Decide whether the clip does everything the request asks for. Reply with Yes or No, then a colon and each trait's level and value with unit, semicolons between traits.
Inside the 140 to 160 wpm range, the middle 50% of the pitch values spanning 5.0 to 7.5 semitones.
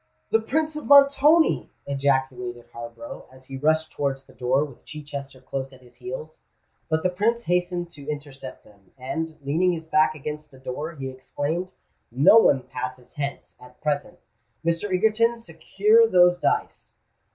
Yes: average, 155 wpm; wide, 5.6 semitones